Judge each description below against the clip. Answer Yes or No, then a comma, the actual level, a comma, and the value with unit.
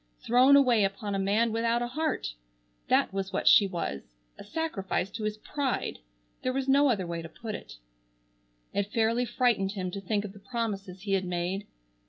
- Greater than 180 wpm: Yes, average, 190 wpm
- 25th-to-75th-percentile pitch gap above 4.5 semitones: No, average, 3.8 semitones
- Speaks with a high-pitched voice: Yes, high, 210 Hz